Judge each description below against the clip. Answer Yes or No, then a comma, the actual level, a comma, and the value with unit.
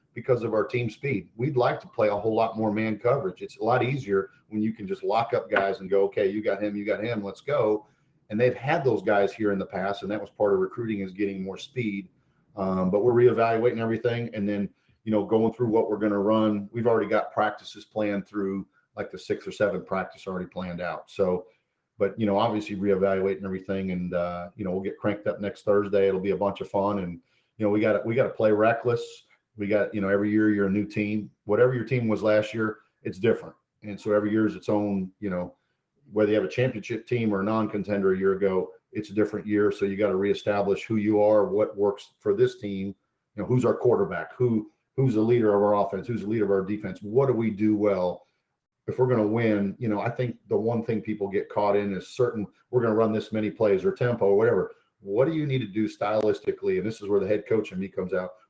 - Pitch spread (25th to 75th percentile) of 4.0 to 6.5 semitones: No, average, 2.7 semitones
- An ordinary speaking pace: No, fast, 255 wpm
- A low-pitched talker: Yes, low, 105 Hz